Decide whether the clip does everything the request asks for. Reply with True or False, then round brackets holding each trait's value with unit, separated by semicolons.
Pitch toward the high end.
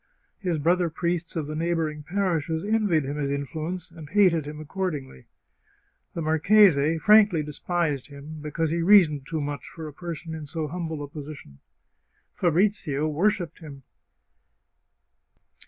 False (160 Hz)